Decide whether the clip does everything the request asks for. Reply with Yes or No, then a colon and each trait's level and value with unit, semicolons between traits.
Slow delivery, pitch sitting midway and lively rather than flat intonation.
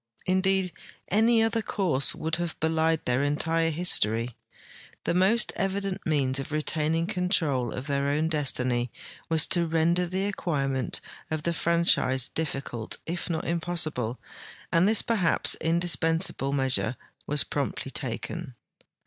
No: slow, 130 wpm; medium, 160 Hz; average, 4.4 semitones